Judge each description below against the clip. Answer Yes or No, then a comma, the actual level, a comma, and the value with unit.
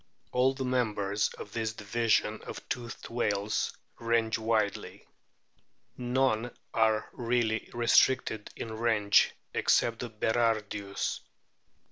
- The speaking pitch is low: Yes, low, 115 Hz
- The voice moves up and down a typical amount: No, narrow, 1.9 semitones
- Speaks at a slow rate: Yes, slow, 105 wpm